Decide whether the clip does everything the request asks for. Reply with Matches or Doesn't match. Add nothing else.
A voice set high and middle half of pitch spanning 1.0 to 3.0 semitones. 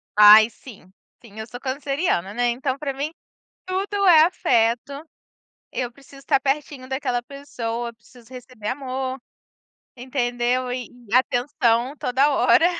Matches